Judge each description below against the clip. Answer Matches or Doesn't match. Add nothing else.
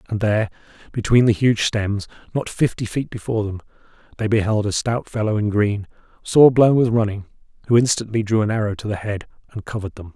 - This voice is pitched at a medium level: Doesn't match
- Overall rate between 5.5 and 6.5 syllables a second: Matches